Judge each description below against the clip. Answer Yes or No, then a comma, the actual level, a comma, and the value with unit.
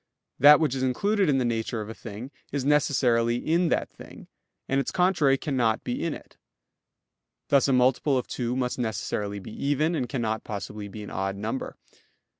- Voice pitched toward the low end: Yes, low, 125 Hz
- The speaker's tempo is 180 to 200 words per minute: Yes, average, 185 wpm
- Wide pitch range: No, average, 4.3 semitones